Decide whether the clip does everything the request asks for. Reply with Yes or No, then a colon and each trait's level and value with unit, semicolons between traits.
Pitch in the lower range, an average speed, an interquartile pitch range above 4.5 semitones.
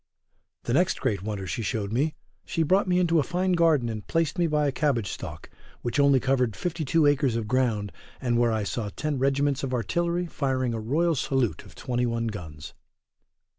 Yes: low, 130 Hz; average, 190 wpm; average, 5.3 semitones